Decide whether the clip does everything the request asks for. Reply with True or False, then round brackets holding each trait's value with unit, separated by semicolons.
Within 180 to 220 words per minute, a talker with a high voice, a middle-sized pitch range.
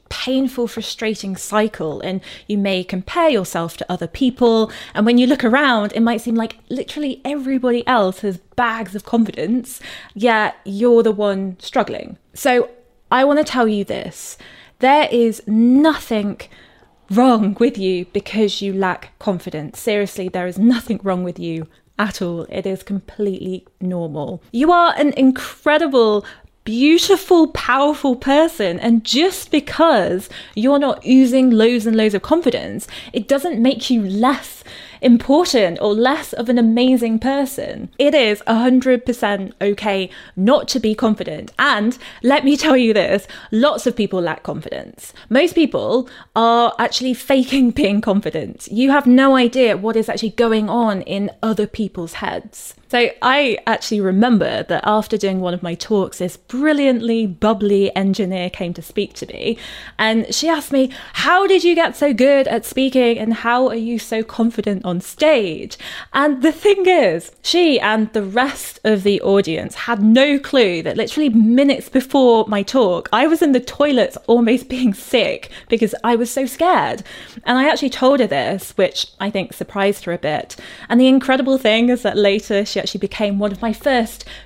False (165 wpm; 230 Hz; 4.4 semitones)